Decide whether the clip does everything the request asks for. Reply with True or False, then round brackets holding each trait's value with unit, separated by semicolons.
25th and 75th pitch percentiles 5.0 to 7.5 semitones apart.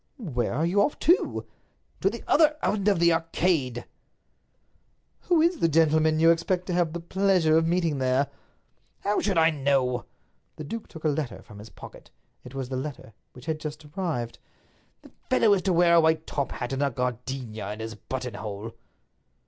True (5.6 semitones)